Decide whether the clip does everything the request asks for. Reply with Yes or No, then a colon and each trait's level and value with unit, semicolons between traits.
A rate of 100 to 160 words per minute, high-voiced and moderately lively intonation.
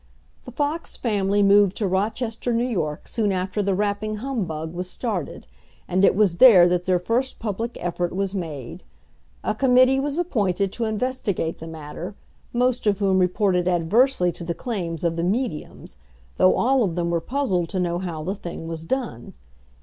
No: average, 175 wpm; high, 195 Hz; average, 4.9 semitones